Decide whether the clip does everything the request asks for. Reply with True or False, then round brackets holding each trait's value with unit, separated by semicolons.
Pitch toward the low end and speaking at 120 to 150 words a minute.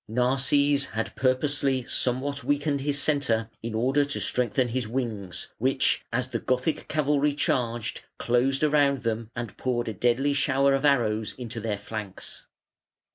True (130 Hz; 145 wpm)